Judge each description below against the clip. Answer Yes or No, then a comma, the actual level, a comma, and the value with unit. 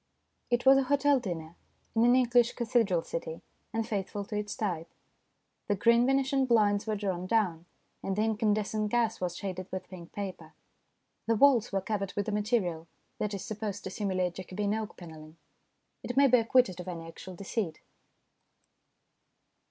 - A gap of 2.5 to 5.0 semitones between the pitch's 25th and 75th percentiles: Yes, average, 3.9 semitones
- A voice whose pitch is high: Yes, high, 205 Hz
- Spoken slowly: No, average, 165 wpm